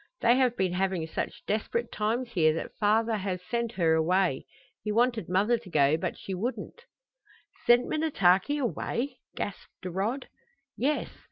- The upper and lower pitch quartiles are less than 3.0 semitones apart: No, average, 4.8 semitones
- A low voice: No, high, 210 Hz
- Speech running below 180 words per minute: Yes, average, 150 wpm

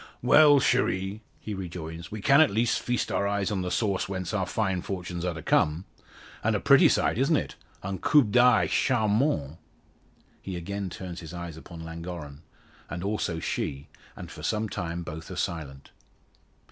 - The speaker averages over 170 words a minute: Yes, average, 180 wpm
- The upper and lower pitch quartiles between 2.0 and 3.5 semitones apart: No, average, 4.3 semitones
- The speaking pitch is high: No, very low, 95 Hz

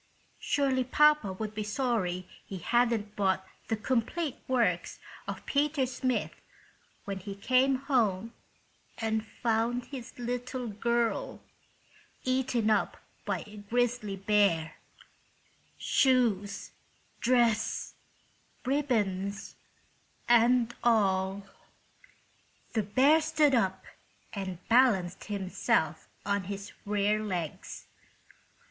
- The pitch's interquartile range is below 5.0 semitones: Yes, average, 4.0 semitones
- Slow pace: Yes, slow, 90 wpm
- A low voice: No, high, 225 Hz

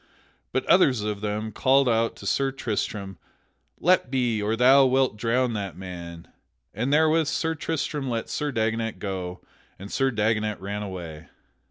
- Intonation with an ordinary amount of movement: Yes, average, 4.6 semitones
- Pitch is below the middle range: Yes, low, 115 Hz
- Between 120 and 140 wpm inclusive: No, average, 155 wpm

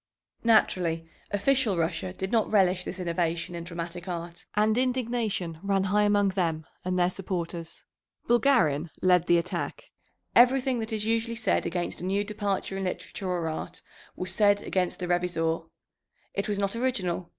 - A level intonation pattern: No, average, 3.5 semitones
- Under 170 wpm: Yes, average, 160 wpm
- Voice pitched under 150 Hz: No, medium, 185 Hz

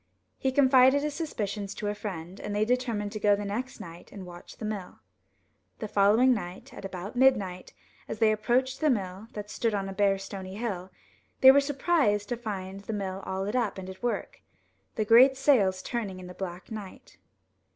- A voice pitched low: No, high, 210 Hz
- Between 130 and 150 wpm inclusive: No, average, 200 wpm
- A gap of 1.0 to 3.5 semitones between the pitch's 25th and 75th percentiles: No, average, 4.1 semitones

